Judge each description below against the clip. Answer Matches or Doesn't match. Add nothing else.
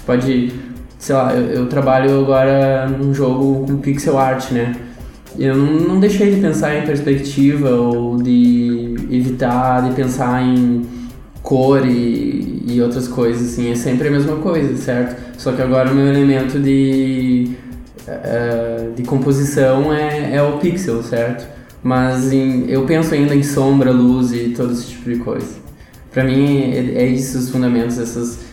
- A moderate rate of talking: Matches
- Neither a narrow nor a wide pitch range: Doesn't match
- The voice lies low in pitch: Matches